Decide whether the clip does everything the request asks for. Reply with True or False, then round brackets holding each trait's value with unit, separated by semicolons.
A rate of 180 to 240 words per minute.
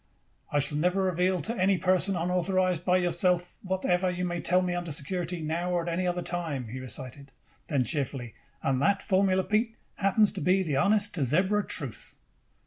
True (185 wpm)